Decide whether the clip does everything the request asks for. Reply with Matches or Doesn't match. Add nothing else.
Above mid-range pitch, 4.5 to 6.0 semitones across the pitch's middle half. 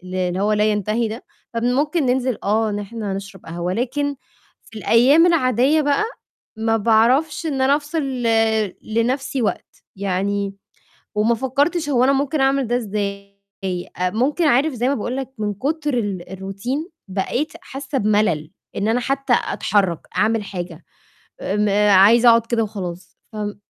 Matches